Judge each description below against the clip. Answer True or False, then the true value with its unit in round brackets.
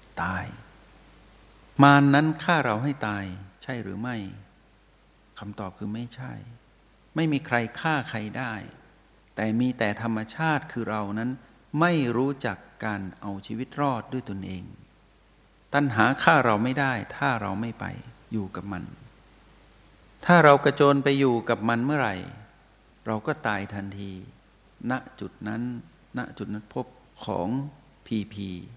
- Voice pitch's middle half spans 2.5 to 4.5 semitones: False (4.9 semitones)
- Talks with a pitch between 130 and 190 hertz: False (115 Hz)